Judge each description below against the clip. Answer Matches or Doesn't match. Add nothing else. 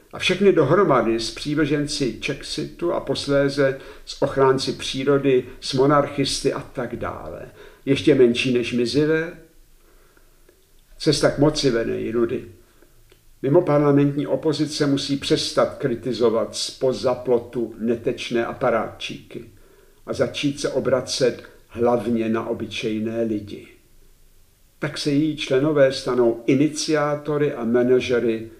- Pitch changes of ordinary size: Matches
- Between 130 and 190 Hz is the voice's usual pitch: Matches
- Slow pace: Matches